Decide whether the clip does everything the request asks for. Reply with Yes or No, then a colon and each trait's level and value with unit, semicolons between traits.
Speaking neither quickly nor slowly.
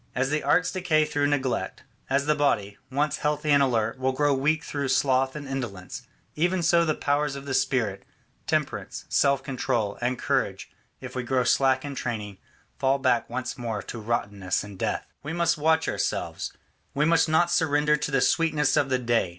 Yes: average, 185 wpm